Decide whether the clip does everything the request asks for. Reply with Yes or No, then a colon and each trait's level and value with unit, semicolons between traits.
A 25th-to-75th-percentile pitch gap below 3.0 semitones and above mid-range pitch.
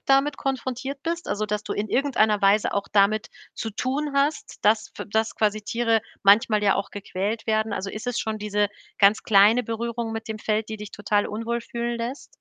Yes: narrow, 2.4 semitones; high, 220 Hz